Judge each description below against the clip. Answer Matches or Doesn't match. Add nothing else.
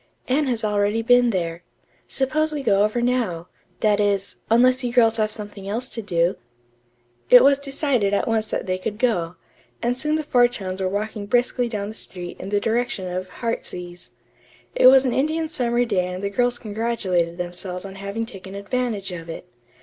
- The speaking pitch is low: Doesn't match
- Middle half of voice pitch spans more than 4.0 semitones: Matches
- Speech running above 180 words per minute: Matches